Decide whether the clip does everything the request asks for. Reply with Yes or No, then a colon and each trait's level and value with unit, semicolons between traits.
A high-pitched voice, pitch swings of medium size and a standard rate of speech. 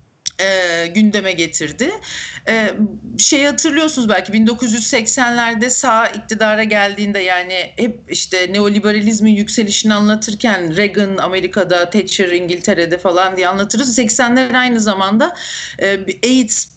Yes: high, 210 Hz; average, 3.7 semitones; average, 105 wpm